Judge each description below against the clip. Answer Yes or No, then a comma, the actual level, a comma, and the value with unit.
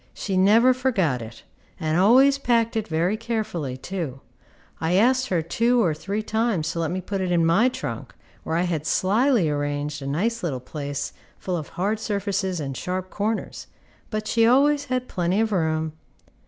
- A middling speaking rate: Yes, average, 180 wpm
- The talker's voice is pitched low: No, medium, 185 Hz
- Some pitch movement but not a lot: No, wide, 6.1 semitones